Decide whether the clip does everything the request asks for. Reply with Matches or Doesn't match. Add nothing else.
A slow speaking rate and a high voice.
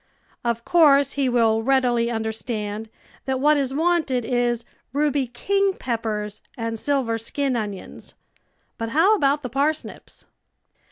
Doesn't match